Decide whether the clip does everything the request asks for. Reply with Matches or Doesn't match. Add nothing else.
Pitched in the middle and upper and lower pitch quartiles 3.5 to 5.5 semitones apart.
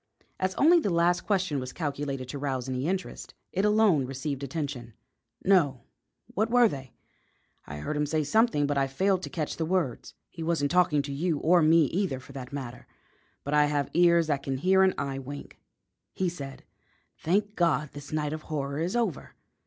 Matches